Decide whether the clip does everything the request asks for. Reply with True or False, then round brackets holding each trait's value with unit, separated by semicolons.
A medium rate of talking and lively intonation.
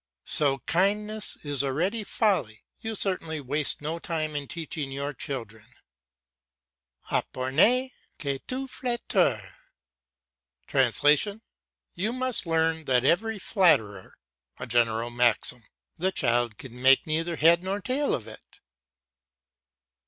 False (110 wpm; 7.0 semitones)